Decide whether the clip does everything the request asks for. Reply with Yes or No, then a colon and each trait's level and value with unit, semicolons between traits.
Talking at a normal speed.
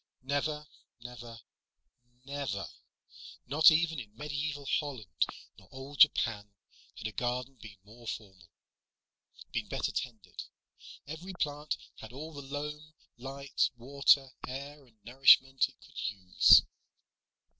No: slow, 115 wpm